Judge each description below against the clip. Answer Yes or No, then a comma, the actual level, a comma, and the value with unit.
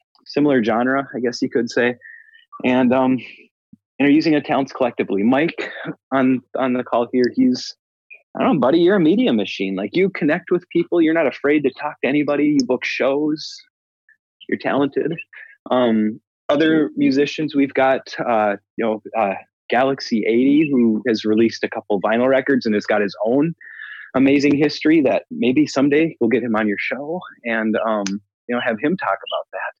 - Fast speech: No, average, 180 wpm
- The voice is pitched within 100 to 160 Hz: Yes, low, 135 Hz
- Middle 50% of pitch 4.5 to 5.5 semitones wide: Yes, average, 4.8 semitones